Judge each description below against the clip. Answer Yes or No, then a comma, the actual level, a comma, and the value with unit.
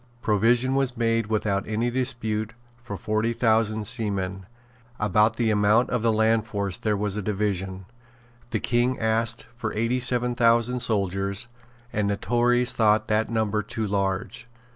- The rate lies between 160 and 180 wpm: No, average, 150 wpm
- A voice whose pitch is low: Yes, low, 110 Hz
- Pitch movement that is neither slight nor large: No, narrow, 2.3 semitones